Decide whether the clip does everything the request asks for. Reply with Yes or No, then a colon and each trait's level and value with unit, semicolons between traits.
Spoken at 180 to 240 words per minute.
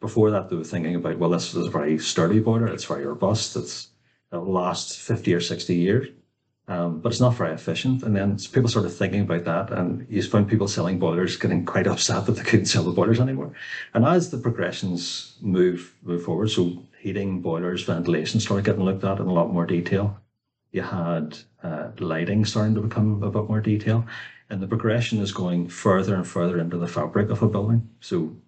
Yes: fast, 205 wpm